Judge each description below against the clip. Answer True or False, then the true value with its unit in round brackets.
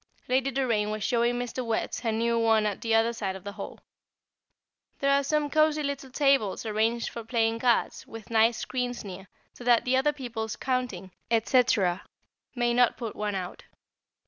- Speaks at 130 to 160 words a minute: False (175 wpm)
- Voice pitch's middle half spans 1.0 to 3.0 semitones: True (2.6 semitones)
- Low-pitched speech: False (235 Hz)